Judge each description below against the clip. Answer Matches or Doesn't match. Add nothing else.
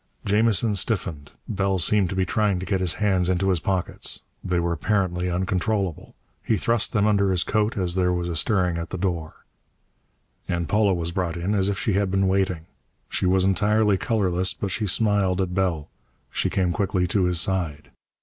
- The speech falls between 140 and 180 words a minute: Doesn't match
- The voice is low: Matches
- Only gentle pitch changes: Matches